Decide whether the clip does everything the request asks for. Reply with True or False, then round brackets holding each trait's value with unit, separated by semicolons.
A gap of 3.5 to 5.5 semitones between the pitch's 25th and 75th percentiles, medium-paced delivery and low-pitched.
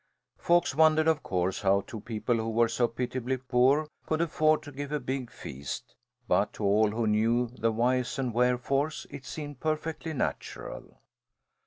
True (4.5 semitones; 165 wpm; 125 Hz)